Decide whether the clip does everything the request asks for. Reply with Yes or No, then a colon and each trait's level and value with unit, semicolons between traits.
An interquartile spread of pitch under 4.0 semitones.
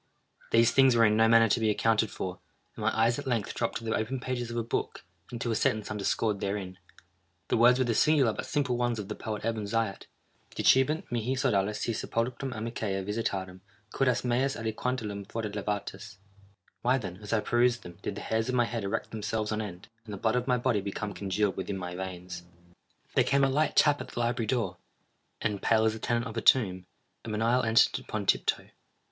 Yes: average, 2.9 semitones